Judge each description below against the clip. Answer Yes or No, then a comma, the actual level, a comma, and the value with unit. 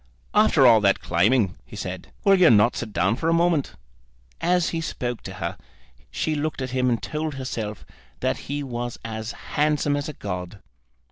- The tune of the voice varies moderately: No, wide, 5.9 semitones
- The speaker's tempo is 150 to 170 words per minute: No, average, 185 wpm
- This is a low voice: Yes, low, 130 Hz